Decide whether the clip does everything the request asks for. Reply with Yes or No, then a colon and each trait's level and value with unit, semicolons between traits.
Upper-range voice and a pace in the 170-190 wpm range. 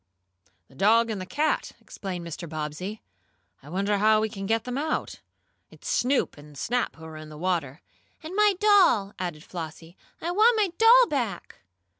Yes: high, 200 Hz; average, 175 wpm